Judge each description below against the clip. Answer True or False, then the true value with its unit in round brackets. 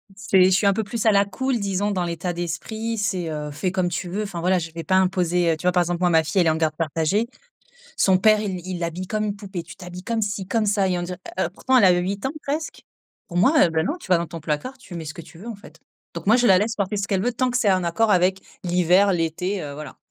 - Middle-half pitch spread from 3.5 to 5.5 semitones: False (3.1 semitones)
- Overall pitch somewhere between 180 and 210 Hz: True (185 Hz)